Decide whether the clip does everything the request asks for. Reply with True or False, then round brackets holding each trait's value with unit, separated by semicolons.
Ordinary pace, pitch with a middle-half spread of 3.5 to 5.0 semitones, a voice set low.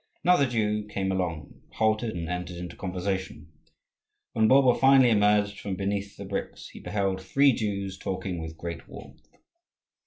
False (150 wpm; 3.1 semitones; 100 Hz)